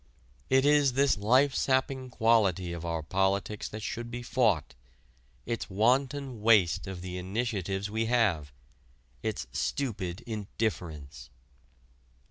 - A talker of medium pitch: No, low, 110 Hz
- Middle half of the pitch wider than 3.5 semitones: Yes, average, 5.1 semitones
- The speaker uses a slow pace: Yes, slow, 115 wpm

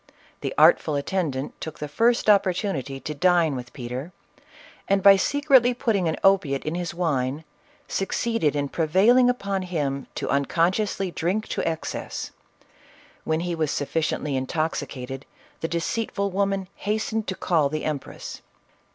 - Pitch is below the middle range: No, medium, 170 Hz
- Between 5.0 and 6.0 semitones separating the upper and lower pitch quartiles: Yes, average, 5.3 semitones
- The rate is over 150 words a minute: No, average, 145 wpm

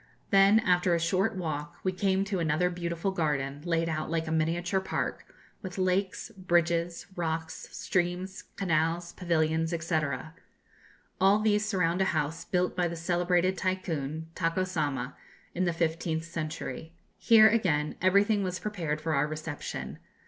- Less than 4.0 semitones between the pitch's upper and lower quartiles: Yes, narrow, 2.6 semitones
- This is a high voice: No, medium, 175 Hz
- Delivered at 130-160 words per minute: Yes, average, 145 wpm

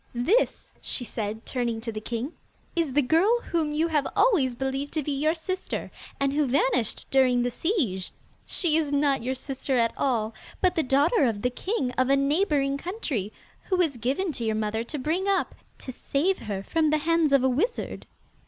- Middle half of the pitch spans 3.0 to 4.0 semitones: No, average, 4.8 semitones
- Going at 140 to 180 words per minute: No, average, 195 wpm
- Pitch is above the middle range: Yes, very high, 275 Hz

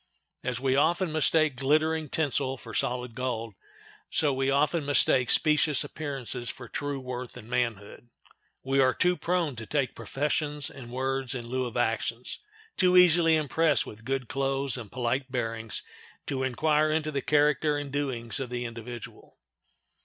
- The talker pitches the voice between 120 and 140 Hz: Yes, low, 135 Hz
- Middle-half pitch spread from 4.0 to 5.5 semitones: No, average, 3.4 semitones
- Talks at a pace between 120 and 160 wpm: Yes, average, 155 wpm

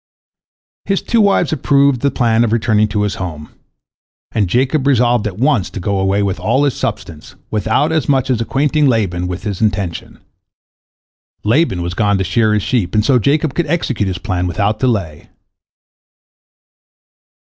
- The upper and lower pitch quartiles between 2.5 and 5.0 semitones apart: No, wide, 5.6 semitones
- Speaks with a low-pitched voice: Yes, low, 110 Hz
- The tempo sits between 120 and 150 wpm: No, average, 165 wpm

